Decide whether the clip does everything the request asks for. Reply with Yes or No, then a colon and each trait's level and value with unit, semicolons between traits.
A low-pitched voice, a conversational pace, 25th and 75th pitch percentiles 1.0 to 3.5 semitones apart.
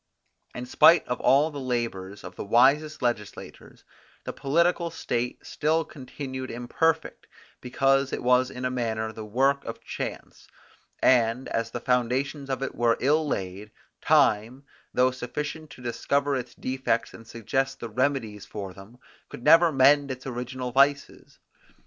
Yes: low, 130 Hz; average, 150 wpm; average, 3.0 semitones